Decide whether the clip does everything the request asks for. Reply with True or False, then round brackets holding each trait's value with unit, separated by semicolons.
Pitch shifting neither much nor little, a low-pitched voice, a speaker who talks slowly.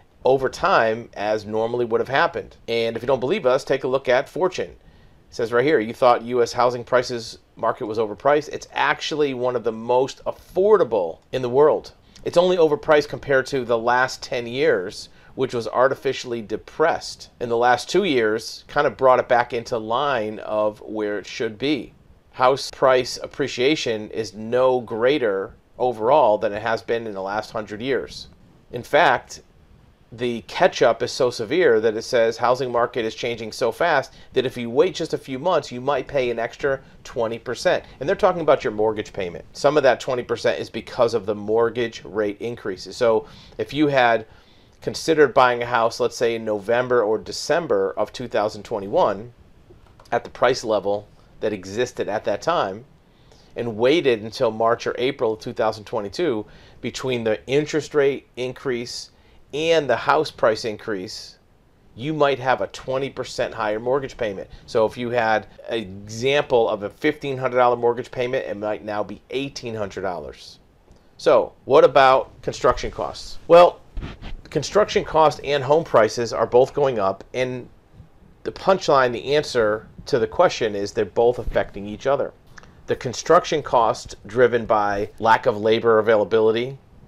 False (3.7 semitones; 120 Hz; 165 wpm)